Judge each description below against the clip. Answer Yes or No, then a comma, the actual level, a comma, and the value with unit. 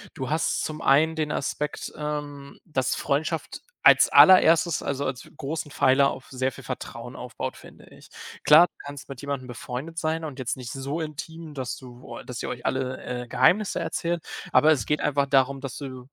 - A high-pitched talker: No, medium, 140 Hz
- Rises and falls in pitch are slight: No, average, 3.2 semitones